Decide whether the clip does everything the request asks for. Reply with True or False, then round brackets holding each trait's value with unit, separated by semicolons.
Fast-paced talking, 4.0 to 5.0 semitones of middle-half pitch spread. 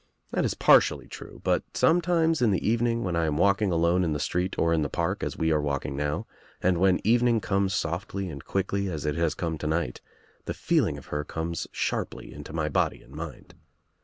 True (215 wpm; 4.4 semitones)